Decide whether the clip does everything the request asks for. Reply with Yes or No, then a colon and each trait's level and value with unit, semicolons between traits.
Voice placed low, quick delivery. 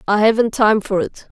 No: high, 215 Hz; fast, 215 wpm